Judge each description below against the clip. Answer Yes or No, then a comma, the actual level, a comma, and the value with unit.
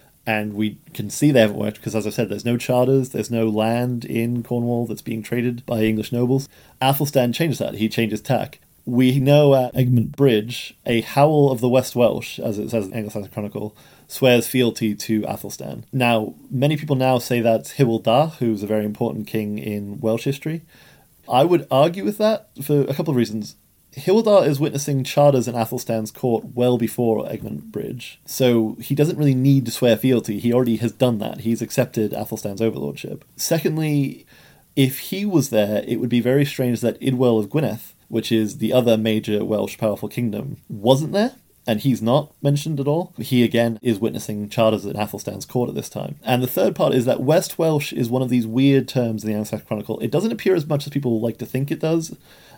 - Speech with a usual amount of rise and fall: Yes, average, 3.6 semitones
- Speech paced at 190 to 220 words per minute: Yes, average, 200 wpm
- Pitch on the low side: Yes, low, 120 Hz